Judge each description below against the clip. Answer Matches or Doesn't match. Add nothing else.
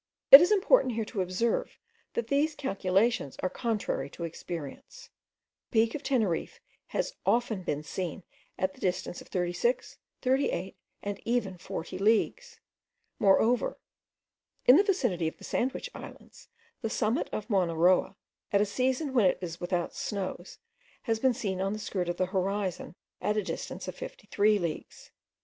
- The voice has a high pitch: Matches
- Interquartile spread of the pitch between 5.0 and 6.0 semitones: Matches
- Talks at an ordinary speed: Matches